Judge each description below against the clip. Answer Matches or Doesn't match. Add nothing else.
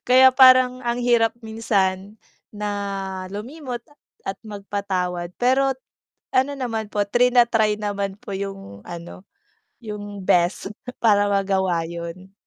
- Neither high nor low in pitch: Doesn't match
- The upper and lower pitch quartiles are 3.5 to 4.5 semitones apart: Matches